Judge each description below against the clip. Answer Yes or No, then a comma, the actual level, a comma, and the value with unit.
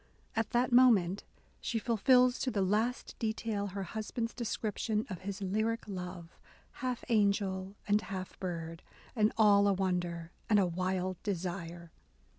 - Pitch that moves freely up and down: No, average, 3.4 semitones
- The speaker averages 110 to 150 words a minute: Yes, average, 140 wpm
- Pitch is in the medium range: No, high, 200 Hz